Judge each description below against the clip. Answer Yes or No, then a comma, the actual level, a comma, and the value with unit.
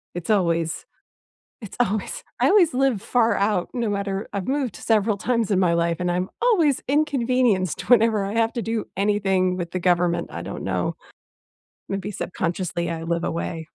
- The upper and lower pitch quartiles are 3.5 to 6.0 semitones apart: Yes, average, 4.6 semitones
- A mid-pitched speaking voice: No, high, 200 Hz